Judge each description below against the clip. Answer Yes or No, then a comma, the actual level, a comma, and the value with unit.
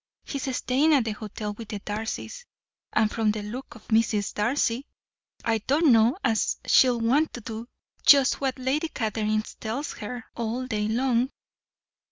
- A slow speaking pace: No, average, 160 wpm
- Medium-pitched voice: No, high, 230 Hz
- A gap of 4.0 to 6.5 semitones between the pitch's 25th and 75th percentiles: No, average, 3.3 semitones